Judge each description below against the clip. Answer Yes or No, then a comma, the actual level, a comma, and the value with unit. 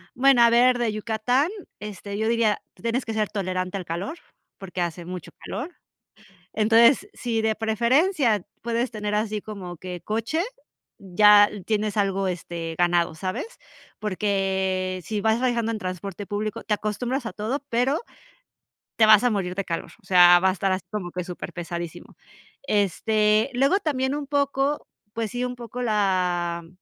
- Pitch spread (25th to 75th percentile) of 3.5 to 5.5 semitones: Yes, average, 4.1 semitones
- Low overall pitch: No, high, 210 Hz